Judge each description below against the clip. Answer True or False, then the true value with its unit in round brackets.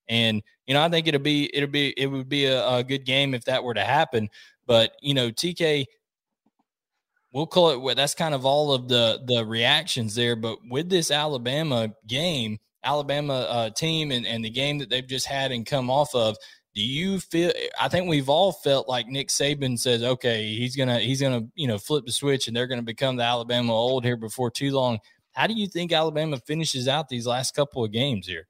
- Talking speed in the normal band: False (225 wpm)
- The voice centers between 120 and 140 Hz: True (130 Hz)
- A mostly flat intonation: False (3.3 semitones)